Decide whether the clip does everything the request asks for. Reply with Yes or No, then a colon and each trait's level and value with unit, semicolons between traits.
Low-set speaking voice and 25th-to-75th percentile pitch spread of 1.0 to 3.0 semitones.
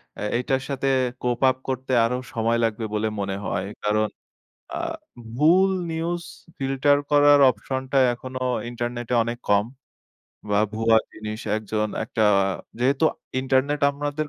No: low, 125 Hz; average, 4.0 semitones